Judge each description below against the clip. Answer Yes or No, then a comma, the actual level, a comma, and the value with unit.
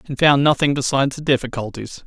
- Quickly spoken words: No, average, 175 wpm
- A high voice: No, low, 135 Hz